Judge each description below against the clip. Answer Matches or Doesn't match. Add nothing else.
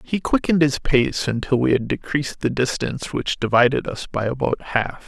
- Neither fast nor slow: Matches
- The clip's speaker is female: Doesn't match